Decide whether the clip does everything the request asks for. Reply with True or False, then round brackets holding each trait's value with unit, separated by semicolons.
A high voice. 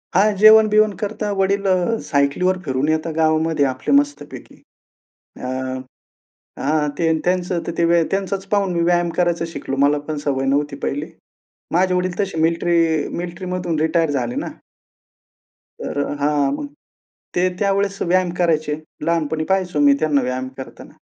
False (170 Hz)